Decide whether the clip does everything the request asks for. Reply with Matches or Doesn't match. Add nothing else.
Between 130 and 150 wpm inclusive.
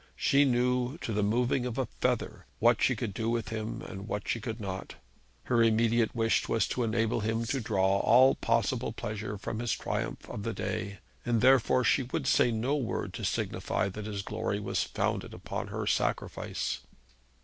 Doesn't match